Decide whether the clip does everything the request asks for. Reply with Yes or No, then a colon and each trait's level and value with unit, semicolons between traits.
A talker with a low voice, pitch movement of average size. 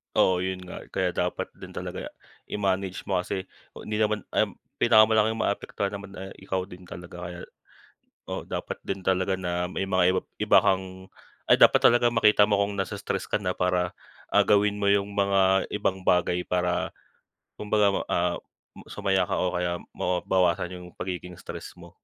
No: very low, 95 Hz; narrow, 2.0 semitones